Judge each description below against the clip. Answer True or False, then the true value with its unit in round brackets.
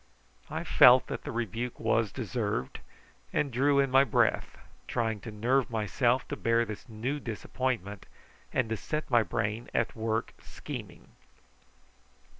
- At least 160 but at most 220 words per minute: False (140 wpm)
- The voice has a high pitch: False (115 Hz)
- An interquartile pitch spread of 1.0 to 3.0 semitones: True (2.6 semitones)